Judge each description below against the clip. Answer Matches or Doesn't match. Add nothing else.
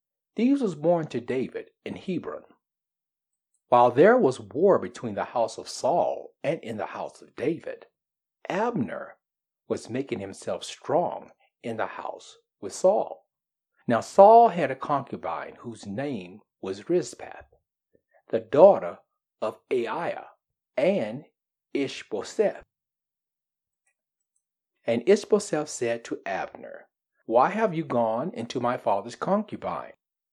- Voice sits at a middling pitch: Matches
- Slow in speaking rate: Matches